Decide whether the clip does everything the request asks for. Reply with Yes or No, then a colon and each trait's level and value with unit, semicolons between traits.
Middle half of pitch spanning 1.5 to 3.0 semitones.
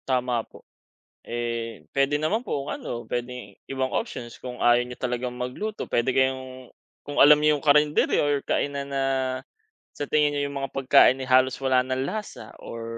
Yes: narrow, 2.6 semitones